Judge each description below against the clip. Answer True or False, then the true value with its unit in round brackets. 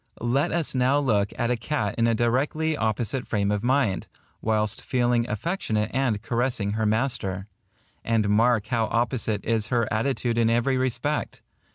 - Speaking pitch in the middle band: False (115 Hz)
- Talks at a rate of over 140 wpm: True (165 wpm)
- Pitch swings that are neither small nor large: True (3.1 semitones)